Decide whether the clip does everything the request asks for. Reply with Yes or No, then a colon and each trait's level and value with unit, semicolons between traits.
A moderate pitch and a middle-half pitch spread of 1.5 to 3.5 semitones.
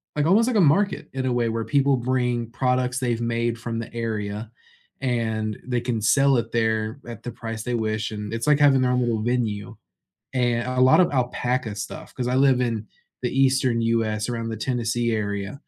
No: low, 120 Hz; narrow, 2.4 semitones